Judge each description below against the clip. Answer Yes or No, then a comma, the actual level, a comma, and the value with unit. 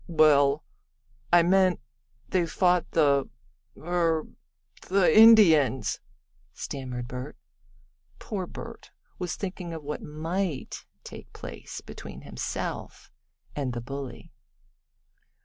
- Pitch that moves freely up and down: No, average, 4.3 semitones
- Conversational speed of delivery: No, slow, 95 wpm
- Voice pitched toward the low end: No, medium, 160 Hz